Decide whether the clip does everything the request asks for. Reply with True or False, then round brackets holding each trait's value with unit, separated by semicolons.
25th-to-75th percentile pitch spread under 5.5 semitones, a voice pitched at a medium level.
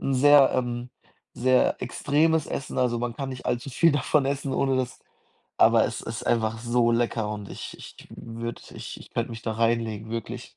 False (2.5 semitones; 120 Hz)